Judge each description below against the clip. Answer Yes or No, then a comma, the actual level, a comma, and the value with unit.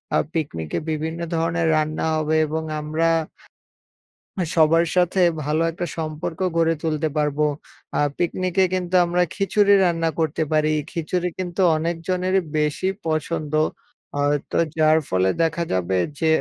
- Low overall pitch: No, medium, 160 Hz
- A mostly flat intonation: Yes, narrow, 2.0 semitones